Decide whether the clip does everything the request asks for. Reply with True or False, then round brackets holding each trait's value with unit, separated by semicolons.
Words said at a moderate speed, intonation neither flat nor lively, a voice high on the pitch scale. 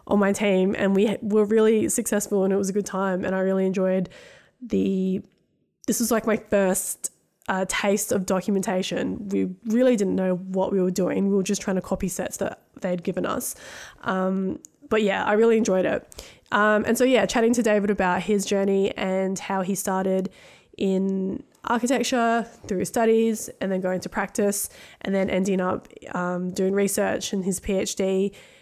False (180 wpm; 2.0 semitones; 195 Hz)